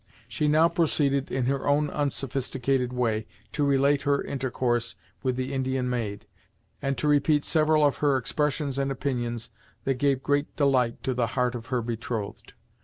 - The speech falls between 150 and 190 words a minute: Yes, average, 165 wpm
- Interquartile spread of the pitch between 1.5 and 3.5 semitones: Yes, narrow, 2.5 semitones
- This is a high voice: No, low, 135 Hz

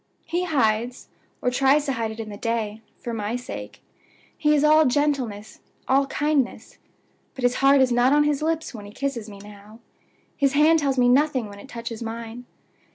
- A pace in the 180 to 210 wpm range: Yes, average, 190 wpm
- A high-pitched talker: Yes, very high, 250 Hz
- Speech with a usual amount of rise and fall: Yes, average, 4.3 semitones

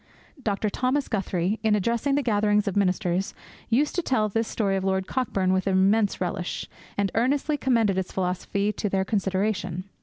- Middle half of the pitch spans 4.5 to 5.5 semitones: No, average, 3.1 semitones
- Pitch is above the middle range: Yes, high, 205 Hz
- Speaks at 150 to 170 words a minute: Yes, average, 160 wpm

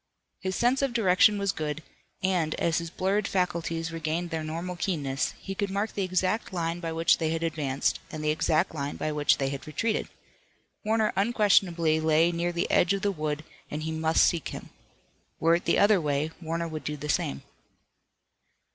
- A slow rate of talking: No, average, 190 wpm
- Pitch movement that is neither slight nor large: Yes, average, 3.4 semitones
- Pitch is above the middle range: No, medium, 165 Hz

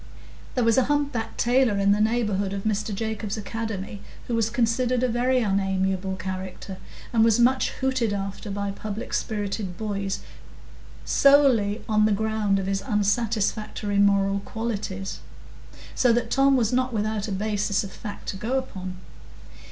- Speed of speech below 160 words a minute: Yes, average, 150 wpm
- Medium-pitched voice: No, high, 215 Hz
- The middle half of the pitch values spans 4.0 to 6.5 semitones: No, average, 2.9 semitones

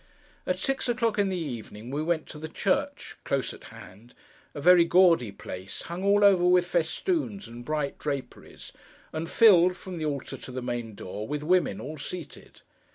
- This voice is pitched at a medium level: Yes, medium, 160 Hz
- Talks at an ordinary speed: Yes, average, 170 wpm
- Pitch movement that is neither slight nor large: No, wide, 6.1 semitones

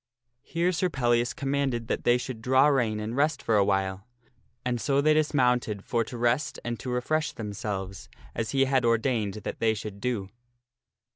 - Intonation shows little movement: No, average, 3.9 semitones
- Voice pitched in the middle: No, low, 120 Hz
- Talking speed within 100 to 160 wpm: No, average, 175 wpm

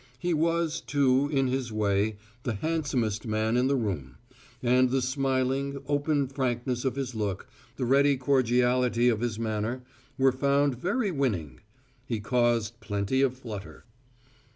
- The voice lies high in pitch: No, low, 125 Hz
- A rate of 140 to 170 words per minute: Yes, average, 145 wpm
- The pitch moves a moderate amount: Yes, average, 3.7 semitones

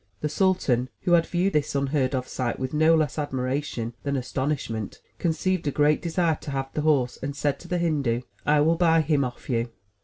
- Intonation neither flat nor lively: Yes, average, 3.7 semitones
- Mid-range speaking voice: Yes, medium, 145 Hz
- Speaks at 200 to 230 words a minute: Yes, fast, 205 wpm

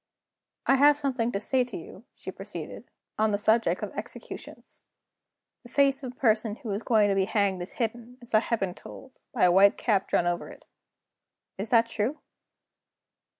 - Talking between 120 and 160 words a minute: No, average, 190 wpm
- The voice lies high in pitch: Yes, high, 225 Hz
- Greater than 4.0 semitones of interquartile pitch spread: No, average, 3.7 semitones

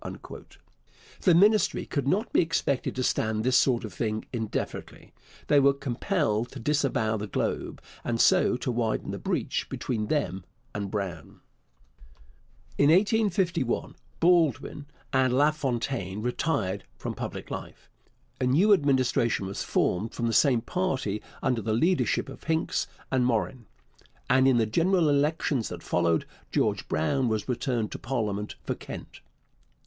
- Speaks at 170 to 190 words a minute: No, average, 140 wpm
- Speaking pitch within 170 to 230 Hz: No, low, 125 Hz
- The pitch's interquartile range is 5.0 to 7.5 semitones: Yes, average, 5.3 semitones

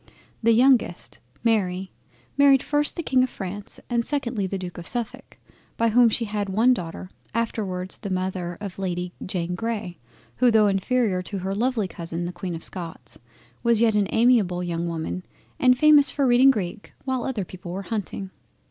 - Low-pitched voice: No, high, 205 Hz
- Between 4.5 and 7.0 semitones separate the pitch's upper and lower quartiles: Yes, average, 4.8 semitones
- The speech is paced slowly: No, average, 175 wpm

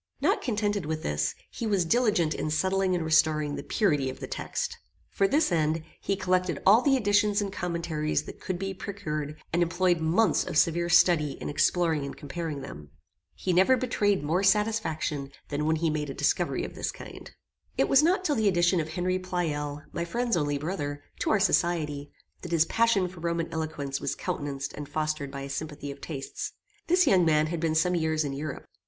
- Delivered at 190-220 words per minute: Yes, average, 195 wpm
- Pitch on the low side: No, medium, 170 Hz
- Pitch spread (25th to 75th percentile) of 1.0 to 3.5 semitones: No, average, 4.2 semitones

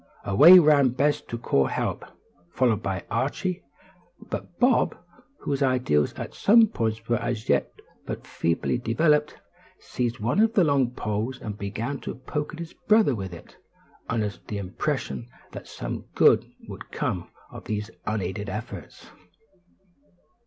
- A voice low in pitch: Yes, low, 120 Hz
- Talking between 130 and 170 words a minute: Yes, average, 145 wpm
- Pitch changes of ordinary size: No, wide, 5.8 semitones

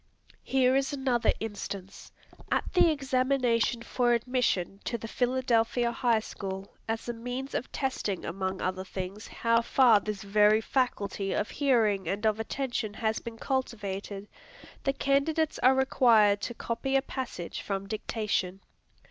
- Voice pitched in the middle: No, high, 230 Hz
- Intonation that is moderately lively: Yes, average, 4.2 semitones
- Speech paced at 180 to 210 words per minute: No, average, 140 wpm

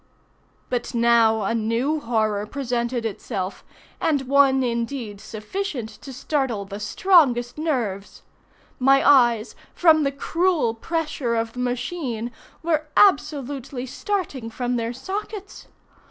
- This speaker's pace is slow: Yes, slow, 115 wpm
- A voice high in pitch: Yes, very high, 250 Hz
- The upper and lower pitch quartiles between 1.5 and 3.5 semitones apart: No, average, 4.2 semitones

